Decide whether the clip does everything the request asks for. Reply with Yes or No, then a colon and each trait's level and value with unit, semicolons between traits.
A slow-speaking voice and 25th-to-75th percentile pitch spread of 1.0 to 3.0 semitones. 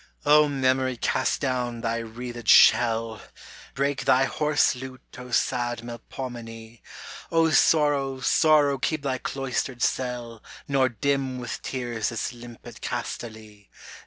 Yes: slow, 120 wpm; narrow, 2.6 semitones